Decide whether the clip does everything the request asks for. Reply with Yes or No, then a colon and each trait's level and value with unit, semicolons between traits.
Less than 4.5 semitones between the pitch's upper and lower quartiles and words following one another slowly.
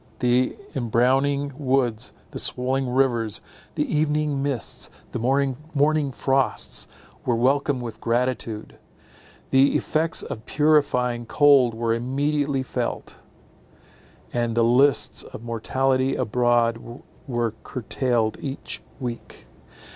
Yes: average, 2.9 semitones; slow, 100 wpm